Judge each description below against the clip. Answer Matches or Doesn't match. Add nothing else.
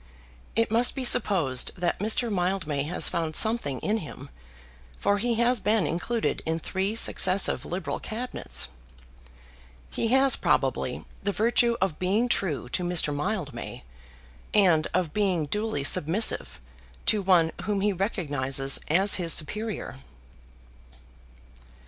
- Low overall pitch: Doesn't match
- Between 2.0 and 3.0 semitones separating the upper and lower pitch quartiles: Doesn't match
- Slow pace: Matches